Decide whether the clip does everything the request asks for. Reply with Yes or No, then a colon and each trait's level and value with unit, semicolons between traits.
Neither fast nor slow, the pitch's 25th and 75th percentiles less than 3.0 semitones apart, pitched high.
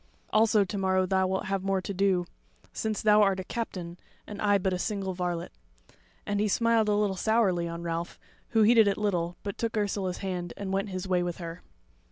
No: fast, 210 wpm; narrow, 2.6 semitones; high, 195 Hz